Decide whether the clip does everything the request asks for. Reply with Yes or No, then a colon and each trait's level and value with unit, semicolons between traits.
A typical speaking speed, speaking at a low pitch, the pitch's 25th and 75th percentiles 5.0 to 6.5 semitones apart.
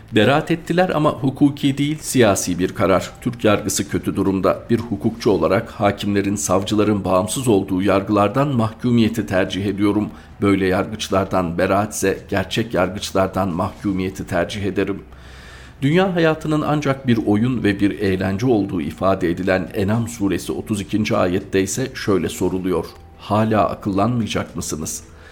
No: average, 125 wpm; low, 100 Hz; average, 3.4 semitones